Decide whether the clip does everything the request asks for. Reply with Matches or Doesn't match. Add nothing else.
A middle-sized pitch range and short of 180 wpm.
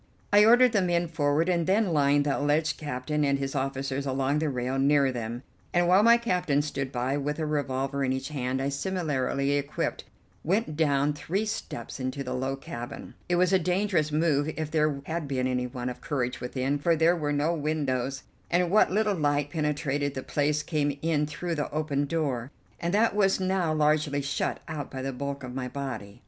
Doesn't match